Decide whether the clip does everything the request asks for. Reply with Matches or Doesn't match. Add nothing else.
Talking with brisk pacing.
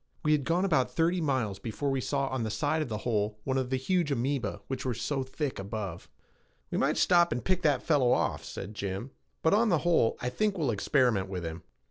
Matches